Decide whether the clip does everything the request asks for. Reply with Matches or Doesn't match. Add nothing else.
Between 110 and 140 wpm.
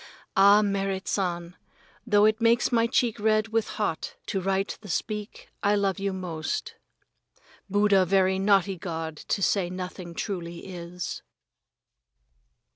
Matches